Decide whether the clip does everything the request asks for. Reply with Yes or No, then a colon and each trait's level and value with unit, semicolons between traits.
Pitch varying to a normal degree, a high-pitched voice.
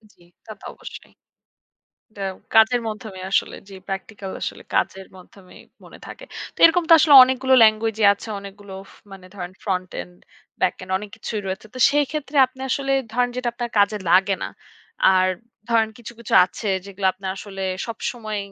Yes: average, 3.9 semitones; high, 210 Hz